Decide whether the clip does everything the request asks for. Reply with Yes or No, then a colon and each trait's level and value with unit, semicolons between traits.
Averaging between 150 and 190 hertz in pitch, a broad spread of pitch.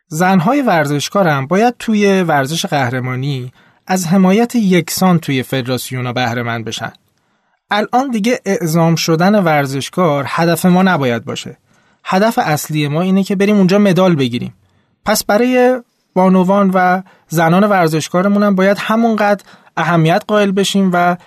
Yes: medium, 185 Hz; wide, 5.7 semitones